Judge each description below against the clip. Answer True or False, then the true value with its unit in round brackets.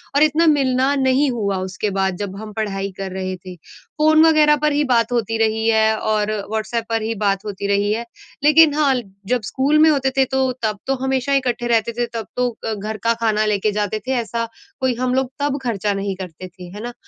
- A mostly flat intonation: False (4.3 semitones)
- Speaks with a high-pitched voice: True (230 Hz)